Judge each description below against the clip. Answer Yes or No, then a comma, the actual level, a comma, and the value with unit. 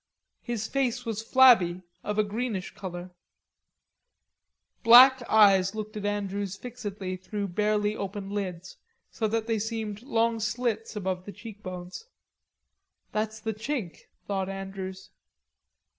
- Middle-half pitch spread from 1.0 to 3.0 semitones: Yes, average, 2.7 semitones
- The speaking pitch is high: Yes, high, 210 Hz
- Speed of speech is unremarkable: No, slow, 120 wpm